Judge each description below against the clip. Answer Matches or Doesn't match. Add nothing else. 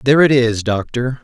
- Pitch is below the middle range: Matches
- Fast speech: Doesn't match